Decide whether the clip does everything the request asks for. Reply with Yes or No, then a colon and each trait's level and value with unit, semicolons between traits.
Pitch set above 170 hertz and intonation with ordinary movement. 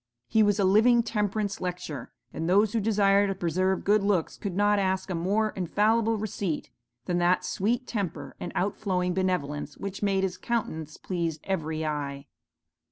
Yes: high, 190 Hz; average, 3.0 semitones